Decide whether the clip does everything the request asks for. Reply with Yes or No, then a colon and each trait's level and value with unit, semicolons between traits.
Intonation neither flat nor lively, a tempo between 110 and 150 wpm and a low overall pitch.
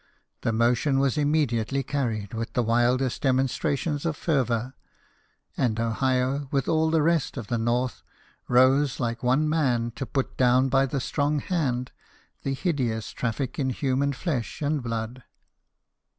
Yes: average, 3.0 semitones; average, 145 wpm; low, 130 Hz